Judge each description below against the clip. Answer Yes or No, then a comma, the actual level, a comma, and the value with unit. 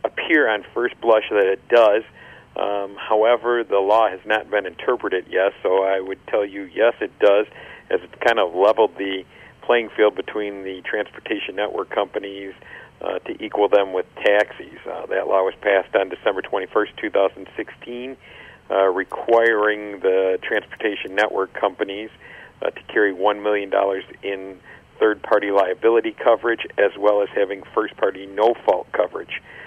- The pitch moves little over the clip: Yes, narrow, 2.0 semitones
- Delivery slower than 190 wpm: Yes, average, 155 wpm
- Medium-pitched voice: No, low, 100 Hz